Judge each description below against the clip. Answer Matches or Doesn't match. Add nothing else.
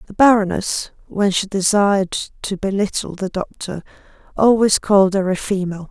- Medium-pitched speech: Doesn't match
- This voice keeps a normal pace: Matches